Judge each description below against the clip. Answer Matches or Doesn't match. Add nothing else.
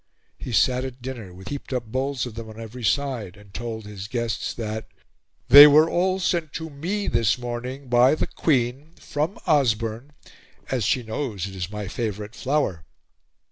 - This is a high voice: Doesn't match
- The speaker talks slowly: Doesn't match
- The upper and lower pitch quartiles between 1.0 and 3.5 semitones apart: Doesn't match